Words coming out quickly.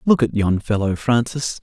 No: average, 185 wpm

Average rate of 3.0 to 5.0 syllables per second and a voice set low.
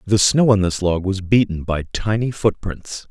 Yes: 4.5 syllables/s; low, 100 Hz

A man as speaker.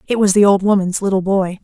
No: female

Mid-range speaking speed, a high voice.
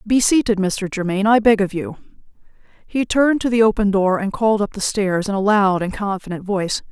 No: fast, 215 wpm; high, 205 Hz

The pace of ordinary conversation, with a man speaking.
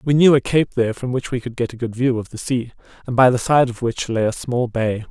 No: fast, 305 wpm; male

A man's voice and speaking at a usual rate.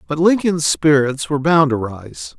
Yes: male; average, 175 wpm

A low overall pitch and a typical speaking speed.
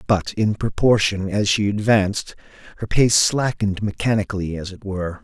Yes: low, 100 Hz; average, 150 wpm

